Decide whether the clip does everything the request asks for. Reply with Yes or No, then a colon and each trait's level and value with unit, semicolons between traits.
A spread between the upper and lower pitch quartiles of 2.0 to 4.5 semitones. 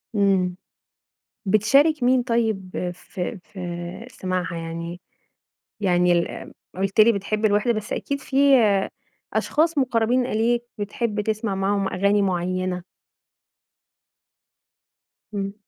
Yes: average, 4.0 semitones